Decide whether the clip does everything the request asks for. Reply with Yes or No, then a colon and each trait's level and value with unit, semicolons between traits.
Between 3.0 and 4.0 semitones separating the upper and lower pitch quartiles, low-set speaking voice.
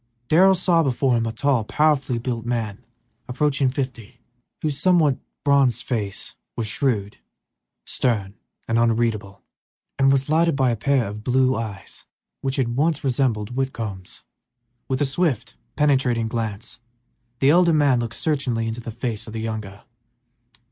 Yes: average, 3.7 semitones; low, 125 Hz